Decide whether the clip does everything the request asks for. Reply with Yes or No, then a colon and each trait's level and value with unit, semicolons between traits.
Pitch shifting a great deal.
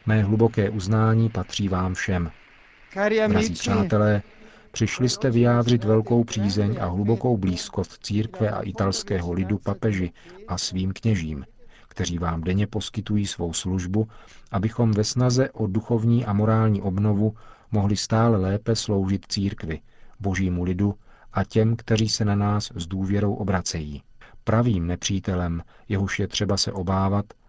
No: average, 2.7 semitones